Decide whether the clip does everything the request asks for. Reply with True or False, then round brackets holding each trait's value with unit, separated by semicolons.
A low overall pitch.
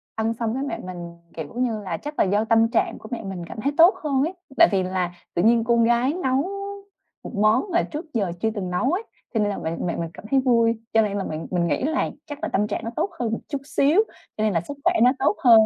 False (225 Hz)